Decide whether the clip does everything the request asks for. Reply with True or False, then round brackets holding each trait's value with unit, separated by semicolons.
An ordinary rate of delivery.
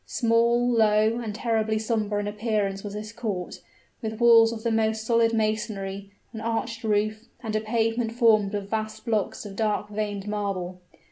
True (165 wpm)